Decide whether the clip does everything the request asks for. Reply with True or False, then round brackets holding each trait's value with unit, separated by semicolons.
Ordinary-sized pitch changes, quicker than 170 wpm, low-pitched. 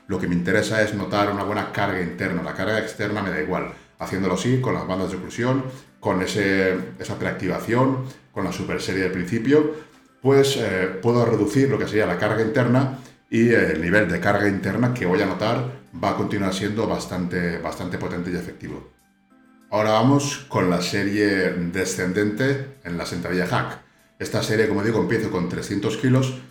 False (5.7 semitones; 185 wpm; 105 Hz)